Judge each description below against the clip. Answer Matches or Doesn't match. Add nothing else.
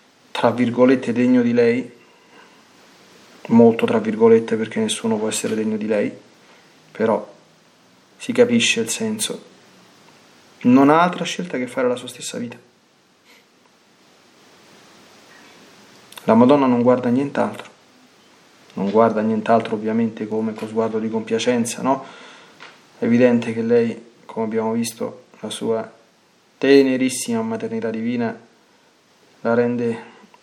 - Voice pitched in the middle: Doesn't match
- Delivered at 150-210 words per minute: Doesn't match